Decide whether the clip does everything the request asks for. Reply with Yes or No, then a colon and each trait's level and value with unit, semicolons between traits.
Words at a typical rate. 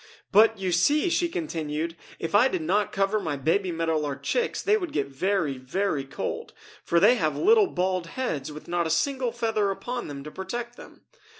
Yes: average, 195 wpm